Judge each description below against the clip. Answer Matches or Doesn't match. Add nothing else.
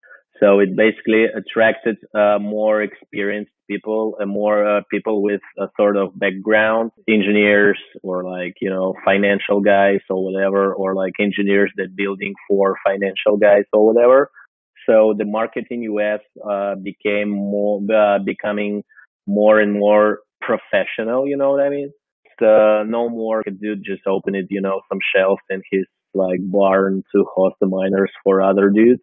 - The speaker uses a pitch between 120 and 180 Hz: Doesn't match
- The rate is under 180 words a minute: Matches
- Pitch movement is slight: Matches